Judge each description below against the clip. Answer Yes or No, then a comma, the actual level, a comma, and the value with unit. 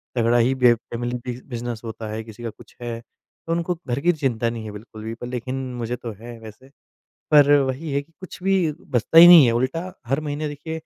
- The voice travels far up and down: No, average, 4.2 semitones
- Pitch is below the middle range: Yes, low, 125 Hz